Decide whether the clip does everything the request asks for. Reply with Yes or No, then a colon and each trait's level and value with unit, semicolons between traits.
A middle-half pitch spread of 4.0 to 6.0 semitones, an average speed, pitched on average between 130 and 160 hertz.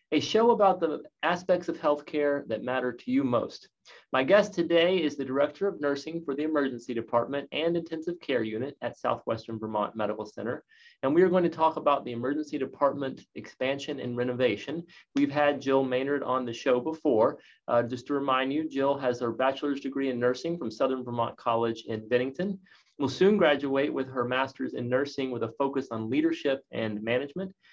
Yes: average, 4.4 semitones; average, 190 wpm; medium, 140 Hz